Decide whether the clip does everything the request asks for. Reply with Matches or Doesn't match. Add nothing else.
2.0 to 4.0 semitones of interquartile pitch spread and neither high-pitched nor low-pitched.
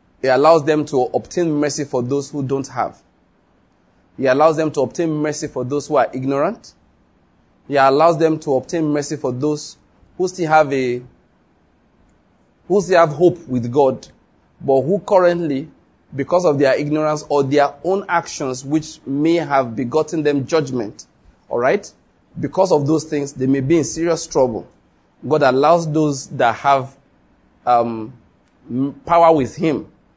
Matches